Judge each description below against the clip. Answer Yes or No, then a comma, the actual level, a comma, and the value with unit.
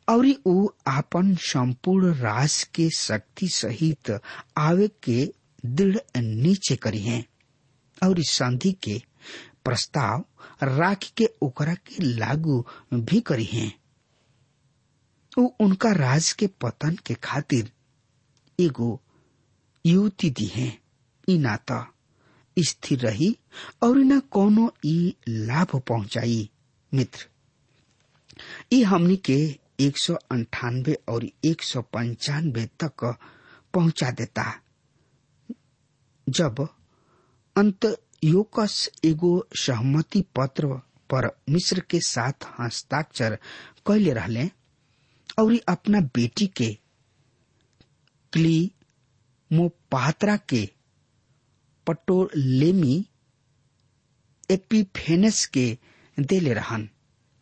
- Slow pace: Yes, slow, 85 wpm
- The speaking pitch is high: No, medium, 140 Hz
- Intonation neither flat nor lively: No, wide, 6.1 semitones